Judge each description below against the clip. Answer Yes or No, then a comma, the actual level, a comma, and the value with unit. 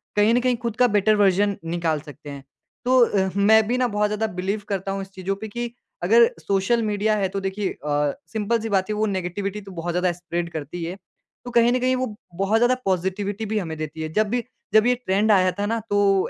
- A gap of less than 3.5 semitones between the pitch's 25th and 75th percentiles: Yes, average, 3.0 semitones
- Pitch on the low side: No, high, 200 Hz